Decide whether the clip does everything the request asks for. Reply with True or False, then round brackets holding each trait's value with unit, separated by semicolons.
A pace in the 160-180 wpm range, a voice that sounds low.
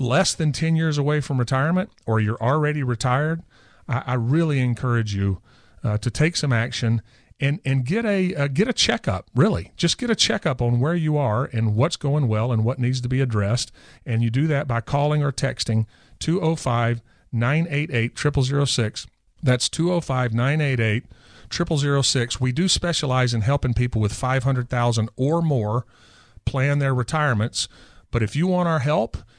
True (165 wpm; 130 Hz)